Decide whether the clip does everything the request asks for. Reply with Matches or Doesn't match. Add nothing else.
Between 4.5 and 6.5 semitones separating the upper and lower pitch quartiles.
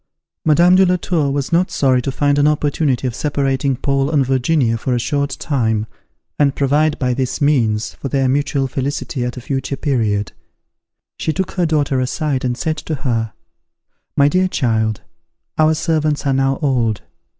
Doesn't match